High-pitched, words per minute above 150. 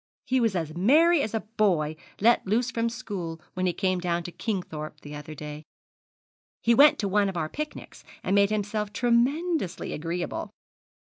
Yes: high, 200 Hz; average, 170 wpm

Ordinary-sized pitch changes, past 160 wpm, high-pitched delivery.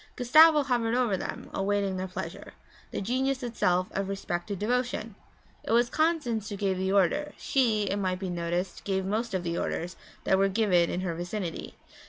Yes: average, 4.5 semitones; average, 180 wpm; high, 200 Hz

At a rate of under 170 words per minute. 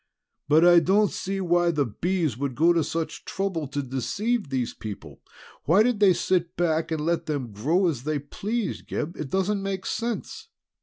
No: average, 185 wpm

